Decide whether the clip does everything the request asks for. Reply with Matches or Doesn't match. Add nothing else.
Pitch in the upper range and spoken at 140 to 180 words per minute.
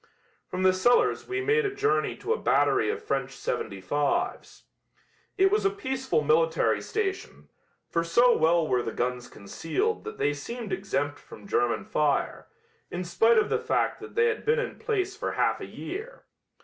Matches